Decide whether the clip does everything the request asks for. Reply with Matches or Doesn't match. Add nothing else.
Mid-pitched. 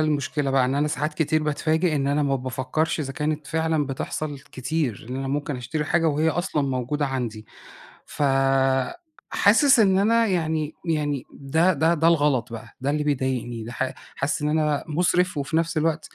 Matches